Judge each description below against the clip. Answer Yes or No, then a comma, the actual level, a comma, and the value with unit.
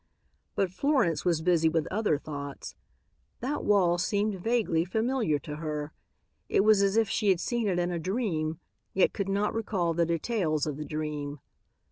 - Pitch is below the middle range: No, medium, 175 Hz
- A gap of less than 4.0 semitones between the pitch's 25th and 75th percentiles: No, average, 5.1 semitones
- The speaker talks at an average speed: Yes, average, 170 wpm